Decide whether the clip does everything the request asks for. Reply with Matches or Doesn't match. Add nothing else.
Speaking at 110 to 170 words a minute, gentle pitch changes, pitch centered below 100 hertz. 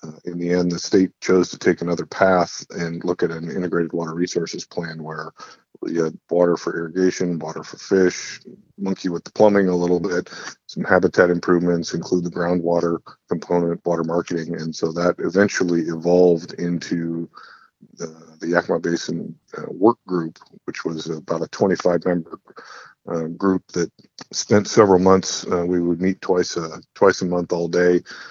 Matches